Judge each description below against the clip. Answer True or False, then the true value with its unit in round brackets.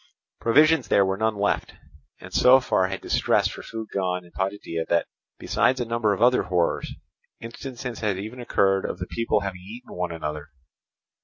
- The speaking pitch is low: True (100 Hz)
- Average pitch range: True (4.1 semitones)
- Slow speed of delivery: False (175 wpm)